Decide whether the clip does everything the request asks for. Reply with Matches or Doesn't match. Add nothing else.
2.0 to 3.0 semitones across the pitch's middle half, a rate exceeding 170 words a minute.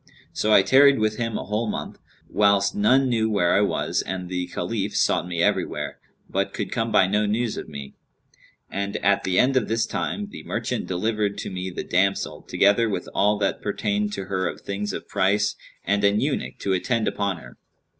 Matches